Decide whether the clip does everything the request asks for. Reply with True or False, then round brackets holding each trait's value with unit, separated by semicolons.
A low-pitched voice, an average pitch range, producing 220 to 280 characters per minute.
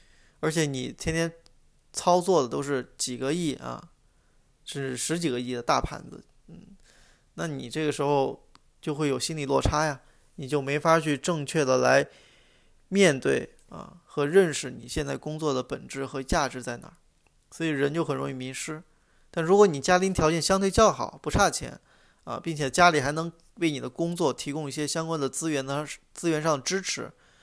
False (150 Hz; 3.3 semitones; 260 characters per minute)